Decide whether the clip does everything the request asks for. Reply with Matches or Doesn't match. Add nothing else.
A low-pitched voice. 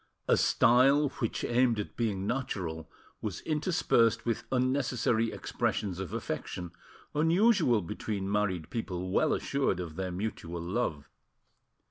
Matches